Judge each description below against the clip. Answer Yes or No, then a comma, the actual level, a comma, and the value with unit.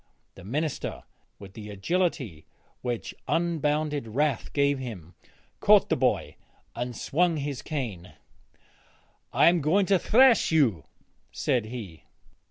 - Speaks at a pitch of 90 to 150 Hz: Yes, medium, 140 Hz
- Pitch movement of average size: No, wide, 6.6 semitones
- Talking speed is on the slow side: Yes, slow, 120 wpm